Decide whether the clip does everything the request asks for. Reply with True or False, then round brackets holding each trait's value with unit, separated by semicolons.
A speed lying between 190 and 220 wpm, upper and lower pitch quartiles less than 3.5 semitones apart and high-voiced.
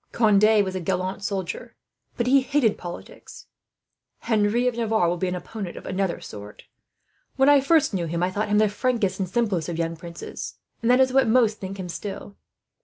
False (195 wpm; 4.5 semitones; 205 Hz)